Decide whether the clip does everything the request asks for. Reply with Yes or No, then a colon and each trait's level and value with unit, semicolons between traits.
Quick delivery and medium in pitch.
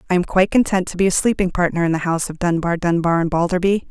Yes: fast, 260 wpm; medium, 175 Hz